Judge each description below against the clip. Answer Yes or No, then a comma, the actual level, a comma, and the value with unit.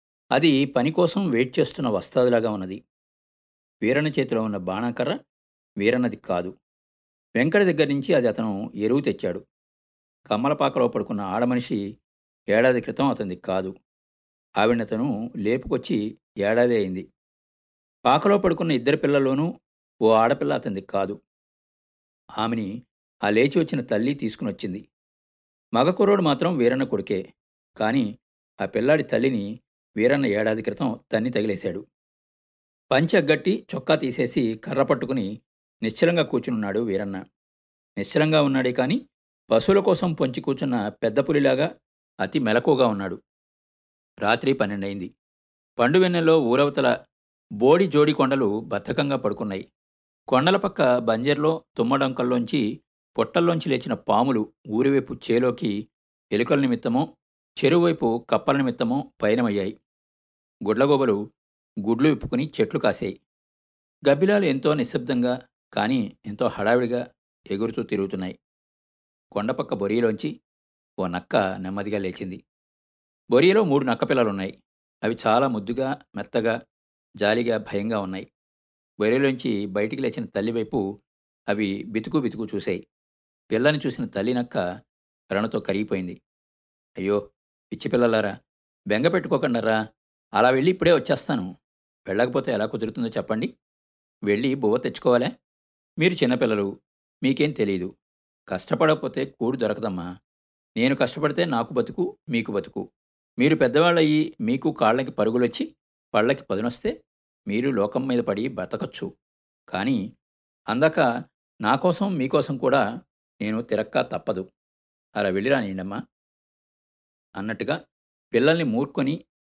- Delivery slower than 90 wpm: No, average, 100 wpm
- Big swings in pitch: Yes, wide, 6.6 semitones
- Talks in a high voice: No, low, 115 Hz